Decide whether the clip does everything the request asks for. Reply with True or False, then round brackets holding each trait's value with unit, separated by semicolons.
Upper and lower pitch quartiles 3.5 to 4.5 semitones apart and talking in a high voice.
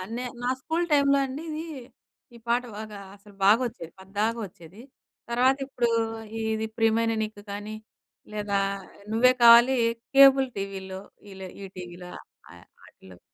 True (4.2 semitones; 220 Hz)